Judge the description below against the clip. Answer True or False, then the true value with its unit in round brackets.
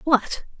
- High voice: True (280 Hz)